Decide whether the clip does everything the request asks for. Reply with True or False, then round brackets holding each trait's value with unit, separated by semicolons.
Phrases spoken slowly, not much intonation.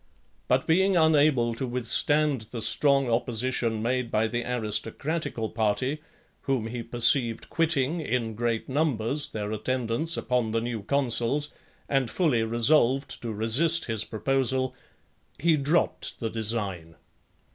False (125 wpm; 4.0 semitones)